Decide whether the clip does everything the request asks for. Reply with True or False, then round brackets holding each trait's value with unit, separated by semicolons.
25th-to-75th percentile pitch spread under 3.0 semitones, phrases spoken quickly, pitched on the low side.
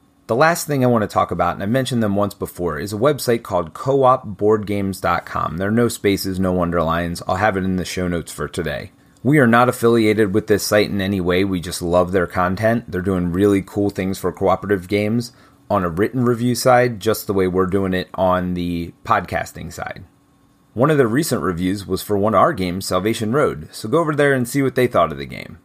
False (4.0 semitones; 225 wpm; 100 Hz)